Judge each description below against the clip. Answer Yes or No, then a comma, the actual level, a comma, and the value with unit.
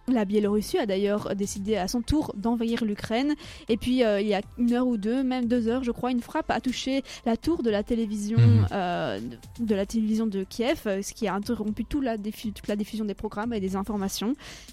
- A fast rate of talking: Yes, fast, 225 wpm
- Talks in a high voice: Yes, high, 220 Hz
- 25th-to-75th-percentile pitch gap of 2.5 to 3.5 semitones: Yes, average, 2.9 semitones